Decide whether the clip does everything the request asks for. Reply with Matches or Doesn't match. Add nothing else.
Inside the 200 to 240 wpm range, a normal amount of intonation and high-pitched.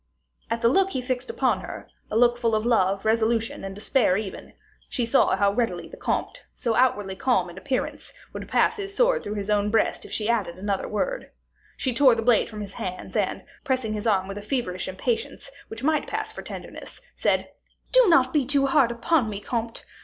Matches